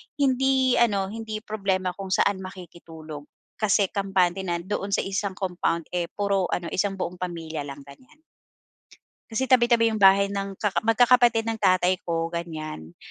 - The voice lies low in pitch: No, high, 195 Hz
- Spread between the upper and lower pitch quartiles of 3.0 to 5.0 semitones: Yes, average, 3.9 semitones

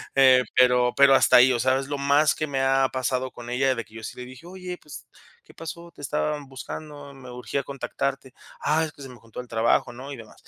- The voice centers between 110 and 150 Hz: Yes, low, 135 Hz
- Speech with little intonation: Yes, narrow, 2.3 semitones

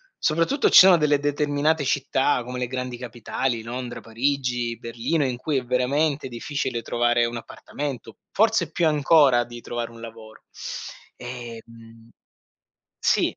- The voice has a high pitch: No, low, 125 Hz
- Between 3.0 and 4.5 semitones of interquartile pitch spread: Yes, average, 3.6 semitones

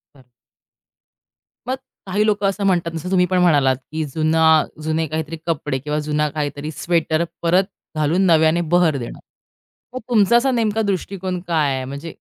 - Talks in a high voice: No, medium, 165 Hz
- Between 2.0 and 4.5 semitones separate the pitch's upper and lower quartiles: Yes, average, 3.7 semitones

